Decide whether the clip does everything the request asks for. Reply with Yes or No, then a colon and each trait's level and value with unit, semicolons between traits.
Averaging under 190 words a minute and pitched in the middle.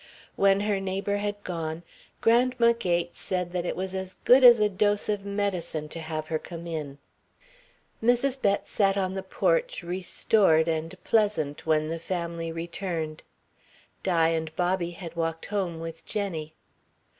Yes: average, 155 wpm; medium, 180 Hz